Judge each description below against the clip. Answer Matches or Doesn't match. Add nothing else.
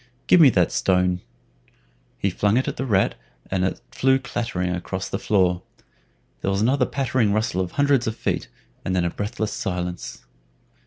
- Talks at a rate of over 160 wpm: Matches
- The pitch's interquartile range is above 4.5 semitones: Matches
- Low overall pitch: Matches